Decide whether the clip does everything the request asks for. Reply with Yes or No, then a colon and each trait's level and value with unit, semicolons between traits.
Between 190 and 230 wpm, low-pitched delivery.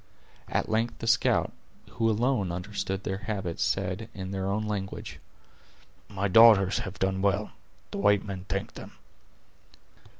No: average, 140 wpm; low, 100 Hz